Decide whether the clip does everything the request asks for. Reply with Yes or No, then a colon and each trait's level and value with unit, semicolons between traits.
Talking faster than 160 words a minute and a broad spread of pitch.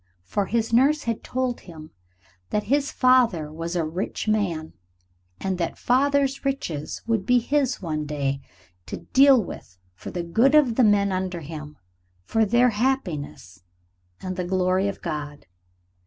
No: average, 155 wpm; wide, 7.5 semitones